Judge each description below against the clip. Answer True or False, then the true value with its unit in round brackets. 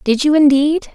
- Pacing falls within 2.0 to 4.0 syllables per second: False (4.7 syllables/s)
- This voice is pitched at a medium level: False (290 Hz)